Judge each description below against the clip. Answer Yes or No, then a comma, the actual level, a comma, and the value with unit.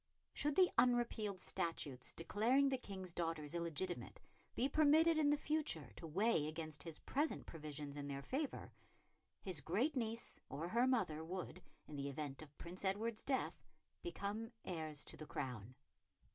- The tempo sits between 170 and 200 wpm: No, average, 155 wpm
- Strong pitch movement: Yes, wide, 8.2 semitones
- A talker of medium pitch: Yes, medium, 180 Hz